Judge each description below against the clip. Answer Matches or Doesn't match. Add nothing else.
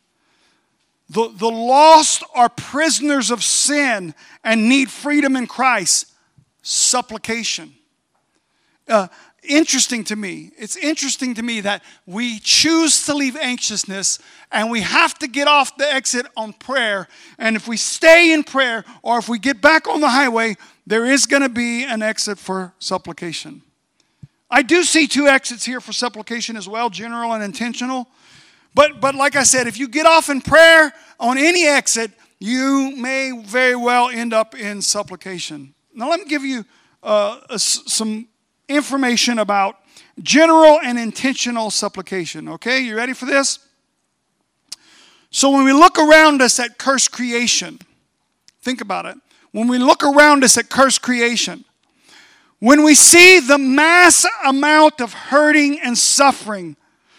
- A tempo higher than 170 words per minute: Doesn't match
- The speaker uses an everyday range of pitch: Matches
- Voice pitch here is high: Matches